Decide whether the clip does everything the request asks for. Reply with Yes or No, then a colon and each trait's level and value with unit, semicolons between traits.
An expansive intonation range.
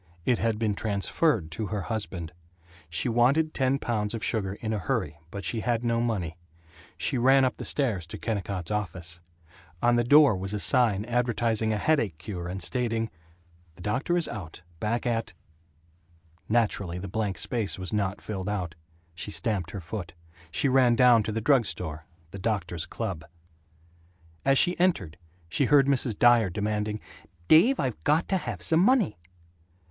No: average, 4.6 semitones